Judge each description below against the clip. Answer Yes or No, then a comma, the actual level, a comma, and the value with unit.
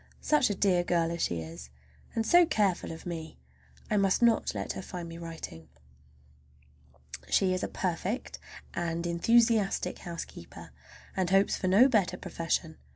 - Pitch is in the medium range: Yes, medium, 180 Hz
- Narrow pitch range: No, average, 3.7 semitones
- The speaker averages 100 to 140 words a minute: No, average, 155 wpm